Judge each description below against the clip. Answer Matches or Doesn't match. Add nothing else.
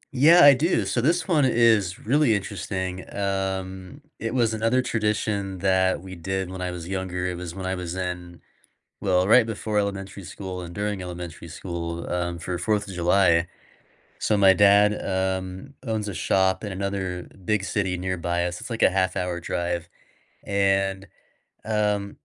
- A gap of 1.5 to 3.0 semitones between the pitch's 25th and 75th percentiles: Matches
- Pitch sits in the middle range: Doesn't match